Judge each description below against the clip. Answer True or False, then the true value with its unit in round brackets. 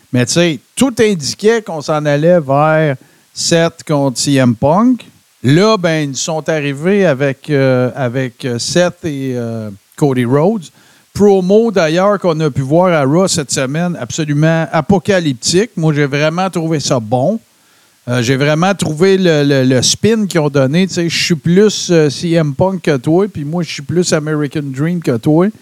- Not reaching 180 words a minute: True (170 wpm)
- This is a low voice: False (160 Hz)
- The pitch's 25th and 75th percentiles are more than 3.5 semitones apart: True (4.5 semitones)